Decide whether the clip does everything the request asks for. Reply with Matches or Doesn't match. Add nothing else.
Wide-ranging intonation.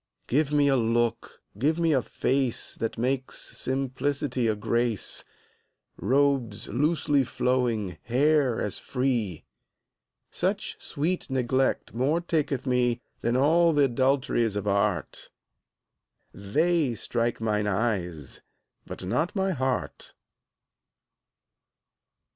Doesn't match